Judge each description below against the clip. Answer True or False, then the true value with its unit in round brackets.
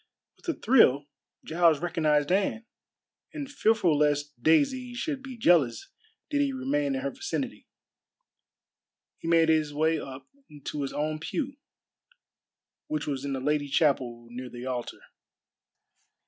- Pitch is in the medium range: True (160 Hz)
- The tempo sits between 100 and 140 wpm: True (135 wpm)